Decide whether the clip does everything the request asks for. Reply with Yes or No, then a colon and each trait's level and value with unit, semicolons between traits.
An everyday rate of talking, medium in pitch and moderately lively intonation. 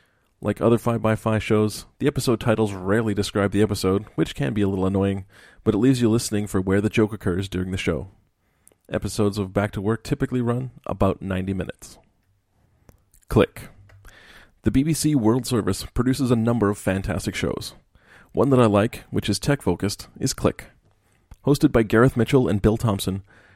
No: average, 175 wpm; low, 105 Hz; average, 3.0 semitones